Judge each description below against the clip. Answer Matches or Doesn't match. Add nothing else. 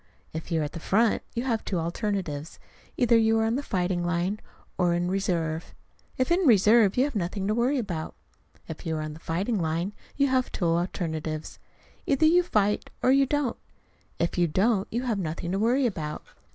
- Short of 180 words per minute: Doesn't match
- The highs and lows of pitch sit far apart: Matches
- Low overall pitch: Doesn't match